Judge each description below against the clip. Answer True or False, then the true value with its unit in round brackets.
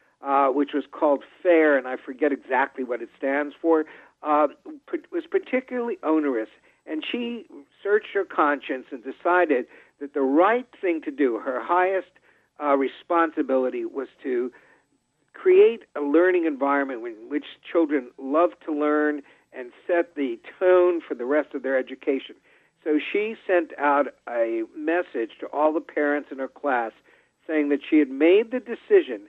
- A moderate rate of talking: True (155 wpm)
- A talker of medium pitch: True (155 Hz)